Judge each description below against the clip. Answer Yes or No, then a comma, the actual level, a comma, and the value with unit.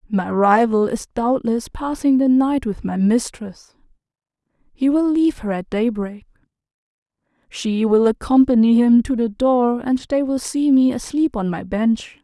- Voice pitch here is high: Yes, high, 240 Hz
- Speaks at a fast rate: No, average, 155 wpm